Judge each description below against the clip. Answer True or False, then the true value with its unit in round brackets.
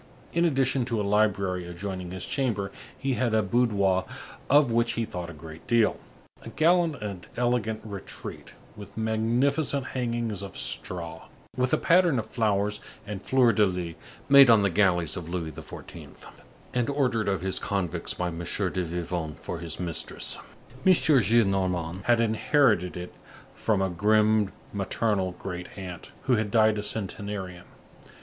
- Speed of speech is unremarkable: True (155 wpm)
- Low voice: True (105 Hz)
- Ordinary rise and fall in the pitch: True (4.5 semitones)